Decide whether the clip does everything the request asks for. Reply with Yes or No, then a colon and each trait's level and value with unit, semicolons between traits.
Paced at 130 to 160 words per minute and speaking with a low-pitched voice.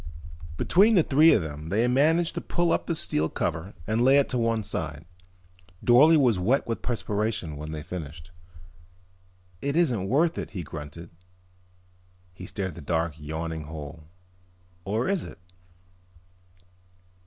Yes: average, 150 wpm; low, 100 Hz